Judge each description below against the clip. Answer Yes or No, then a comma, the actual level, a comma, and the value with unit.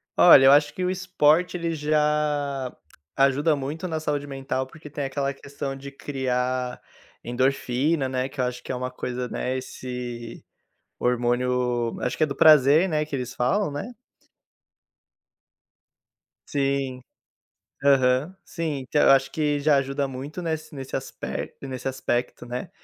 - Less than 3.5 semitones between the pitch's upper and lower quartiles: Yes, average, 2.8 semitones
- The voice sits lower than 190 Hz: Yes, low, 135 Hz